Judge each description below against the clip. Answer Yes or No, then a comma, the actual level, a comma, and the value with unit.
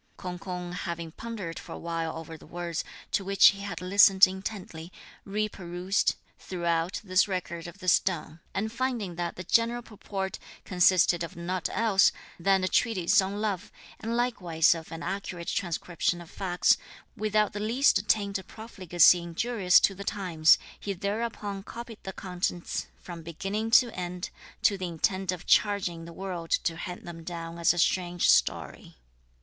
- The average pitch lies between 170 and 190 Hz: Yes, medium, 185 Hz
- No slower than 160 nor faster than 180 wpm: Yes, average, 165 wpm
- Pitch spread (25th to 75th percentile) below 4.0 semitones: Yes, average, 2.8 semitones